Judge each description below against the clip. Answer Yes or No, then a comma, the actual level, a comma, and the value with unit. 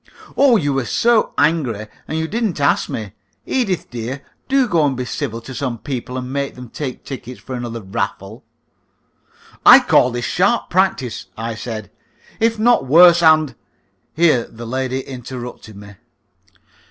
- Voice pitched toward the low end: Yes, low, 130 Hz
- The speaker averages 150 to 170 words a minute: Yes, average, 165 wpm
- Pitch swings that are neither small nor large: No, wide, 5.8 semitones